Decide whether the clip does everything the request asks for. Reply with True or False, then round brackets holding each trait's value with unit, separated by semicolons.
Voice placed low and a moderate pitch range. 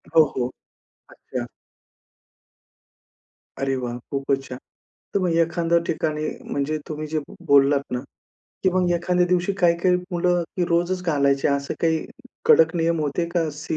False (160 Hz; 3.8 semitones)